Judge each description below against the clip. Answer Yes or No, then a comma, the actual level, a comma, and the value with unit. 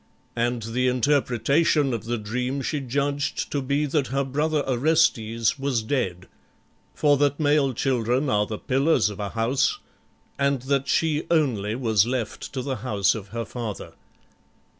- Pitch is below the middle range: Yes, low, 130 Hz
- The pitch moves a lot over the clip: No, average, 3.8 semitones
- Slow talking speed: No, average, 155 wpm